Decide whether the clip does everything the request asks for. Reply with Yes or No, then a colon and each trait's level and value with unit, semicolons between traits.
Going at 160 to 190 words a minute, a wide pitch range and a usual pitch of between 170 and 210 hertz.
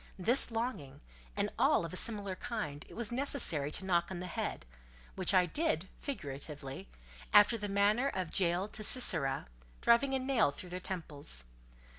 Yes: average, 165 wpm; wide, 6.6 semitones; high, 190 Hz